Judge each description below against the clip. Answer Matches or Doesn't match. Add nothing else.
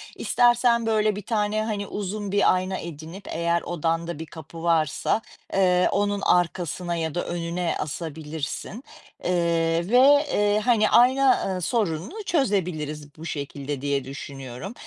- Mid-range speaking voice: Matches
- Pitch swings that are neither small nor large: Matches